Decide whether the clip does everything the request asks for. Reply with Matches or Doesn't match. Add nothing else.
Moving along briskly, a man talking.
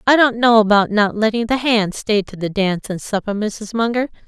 Doesn't match